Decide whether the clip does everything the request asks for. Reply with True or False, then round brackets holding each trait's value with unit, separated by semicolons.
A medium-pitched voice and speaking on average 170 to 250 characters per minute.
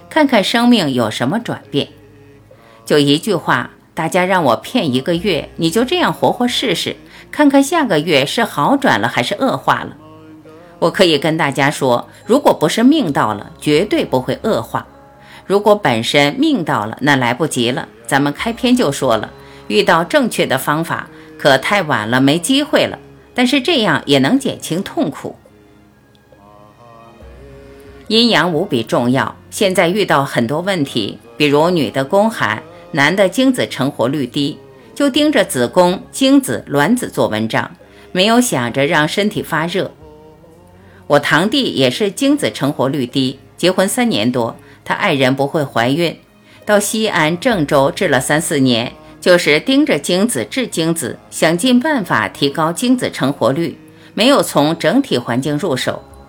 True (150 Hz; 230 characters per minute)